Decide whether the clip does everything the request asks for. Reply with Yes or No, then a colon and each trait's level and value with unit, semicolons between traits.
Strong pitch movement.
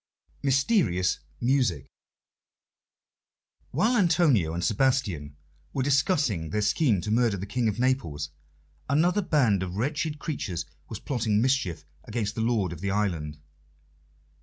Yes: wide, 6.9 semitones